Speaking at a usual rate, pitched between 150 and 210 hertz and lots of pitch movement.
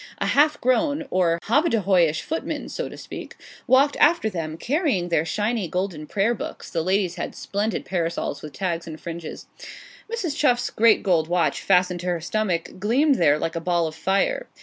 Yes: average, 175 wpm; high, 190 Hz; wide, 6.5 semitones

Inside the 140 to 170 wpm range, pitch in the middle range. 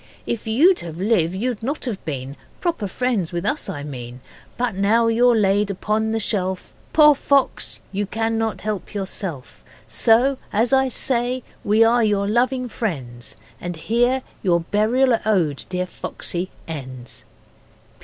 No: average, 150 wpm; high, 215 Hz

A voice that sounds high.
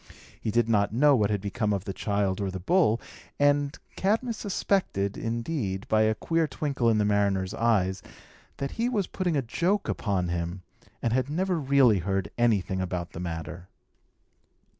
No: low, 110 Hz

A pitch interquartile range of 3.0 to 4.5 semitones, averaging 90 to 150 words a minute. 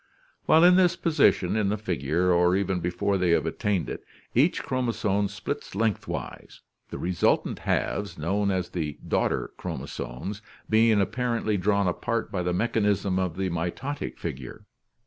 Yes: average, 3.5 semitones; average, 145 wpm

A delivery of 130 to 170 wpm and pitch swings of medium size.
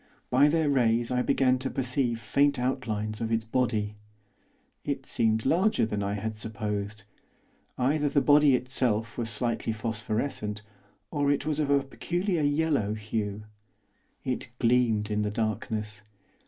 Yes: average, 140 wpm; average, 4.4 semitones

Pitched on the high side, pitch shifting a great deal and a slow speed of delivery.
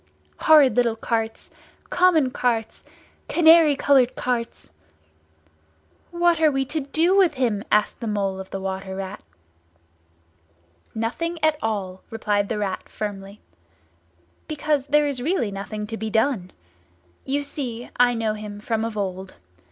Yes: high, 230 Hz; wide, 5.8 semitones; slow, 130 wpm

